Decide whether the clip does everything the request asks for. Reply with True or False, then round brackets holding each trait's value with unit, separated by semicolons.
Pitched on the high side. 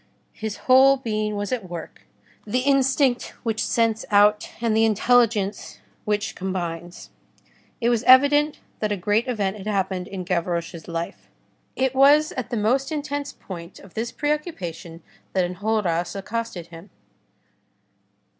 True (215 Hz)